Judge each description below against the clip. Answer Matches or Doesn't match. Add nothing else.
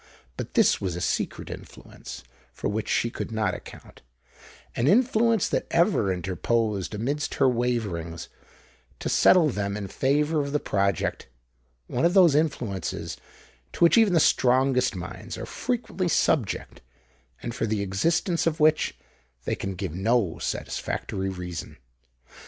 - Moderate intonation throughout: Doesn't match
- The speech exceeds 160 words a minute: Doesn't match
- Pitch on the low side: Matches